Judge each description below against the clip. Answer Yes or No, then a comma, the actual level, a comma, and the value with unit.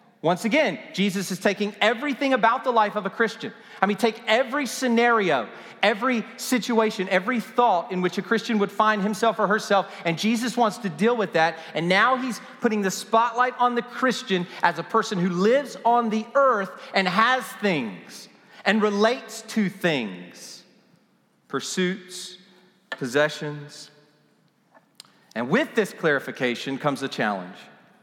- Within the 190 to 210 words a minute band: No, average, 150 wpm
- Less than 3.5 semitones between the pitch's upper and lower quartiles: No, average, 4.3 semitones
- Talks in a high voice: Yes, high, 210 Hz